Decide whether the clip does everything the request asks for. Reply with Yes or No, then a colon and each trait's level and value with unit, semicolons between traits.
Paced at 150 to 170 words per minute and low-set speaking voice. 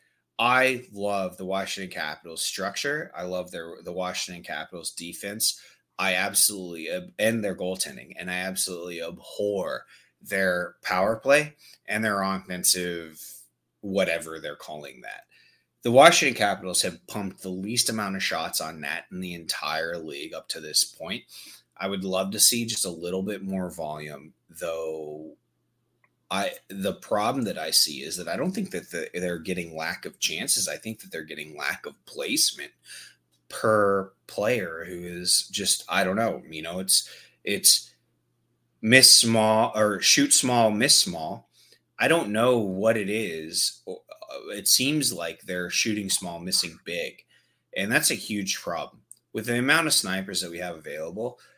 Yes: average, 160 wpm; very low, 95 Hz